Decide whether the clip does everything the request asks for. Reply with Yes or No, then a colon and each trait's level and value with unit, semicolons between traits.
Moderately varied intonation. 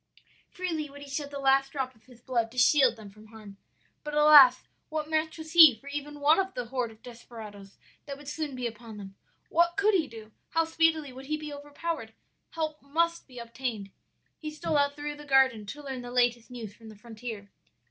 Yes: average, 4.6 semitones